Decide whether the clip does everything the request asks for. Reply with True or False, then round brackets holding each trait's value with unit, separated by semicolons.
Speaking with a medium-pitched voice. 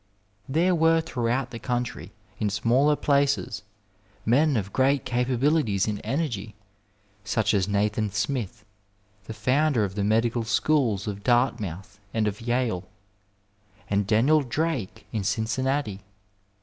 False (115 Hz)